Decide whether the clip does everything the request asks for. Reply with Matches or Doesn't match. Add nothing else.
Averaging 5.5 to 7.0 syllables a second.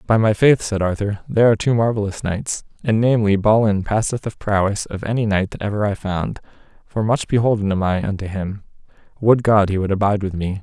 Matches